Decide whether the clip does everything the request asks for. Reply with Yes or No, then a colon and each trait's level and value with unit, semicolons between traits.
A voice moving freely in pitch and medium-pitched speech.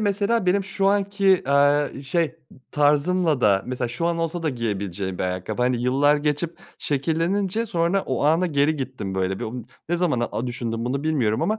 Yes: wide, 6.2 semitones; medium, 145 Hz